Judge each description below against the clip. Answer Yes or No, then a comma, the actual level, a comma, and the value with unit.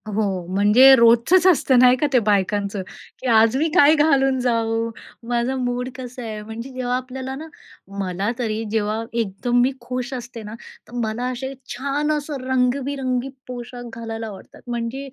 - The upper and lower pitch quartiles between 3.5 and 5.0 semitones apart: No, average, 2.7 semitones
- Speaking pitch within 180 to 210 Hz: No, high, 245 Hz